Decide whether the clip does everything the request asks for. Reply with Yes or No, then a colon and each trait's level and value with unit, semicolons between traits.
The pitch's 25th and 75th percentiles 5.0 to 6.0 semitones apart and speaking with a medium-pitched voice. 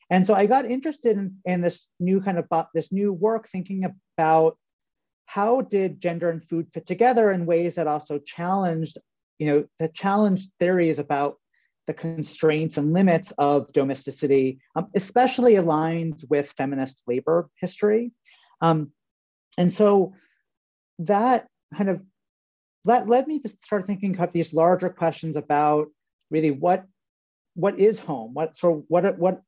No: average, 4.2 semitones; medium, 175 Hz